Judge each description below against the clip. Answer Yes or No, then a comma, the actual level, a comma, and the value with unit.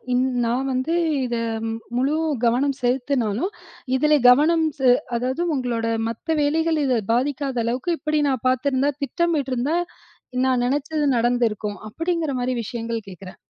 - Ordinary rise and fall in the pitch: Yes, average, 3.6 semitones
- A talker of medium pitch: No, very high, 260 Hz